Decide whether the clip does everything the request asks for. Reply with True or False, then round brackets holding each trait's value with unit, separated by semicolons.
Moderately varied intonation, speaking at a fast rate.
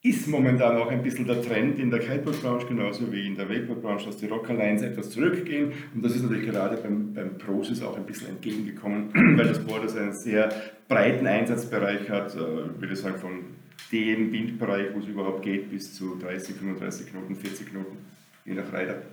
True (3.1 semitones; 195 wpm)